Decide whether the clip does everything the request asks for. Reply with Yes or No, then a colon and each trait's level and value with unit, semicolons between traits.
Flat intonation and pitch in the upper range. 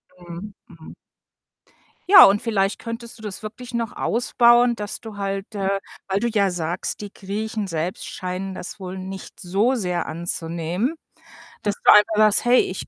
No: average, 3.2 semitones; high, 200 Hz